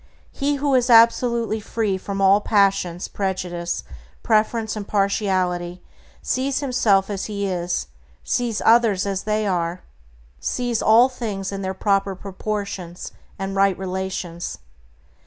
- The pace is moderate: No, slow, 125 wpm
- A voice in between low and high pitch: No, high, 200 Hz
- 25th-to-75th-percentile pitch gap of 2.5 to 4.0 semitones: Yes, average, 3.0 semitones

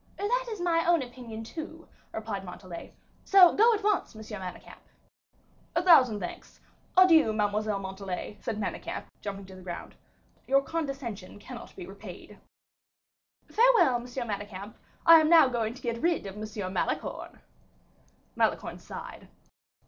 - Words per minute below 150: Yes, average, 140 wpm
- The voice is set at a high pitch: Yes, high, 235 Hz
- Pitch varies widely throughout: Yes, wide, 8.3 semitones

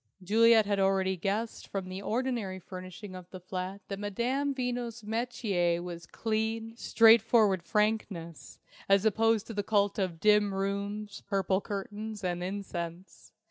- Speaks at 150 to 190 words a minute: No, average, 140 wpm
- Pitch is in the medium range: No, high, 200 Hz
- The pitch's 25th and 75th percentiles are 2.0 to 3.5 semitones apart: Yes, average, 2.9 semitones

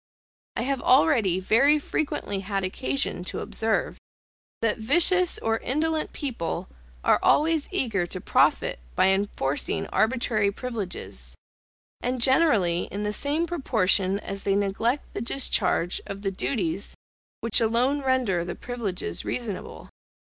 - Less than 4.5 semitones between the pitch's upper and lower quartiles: No, wide, 5.4 semitones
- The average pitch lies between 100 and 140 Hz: No, high, 220 Hz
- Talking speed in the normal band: No, slow, 125 wpm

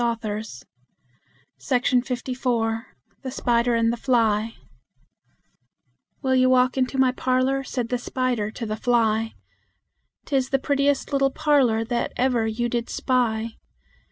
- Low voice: No, high, 245 Hz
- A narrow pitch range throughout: Yes, narrow, 2.3 semitones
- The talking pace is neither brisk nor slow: No, slow, 130 wpm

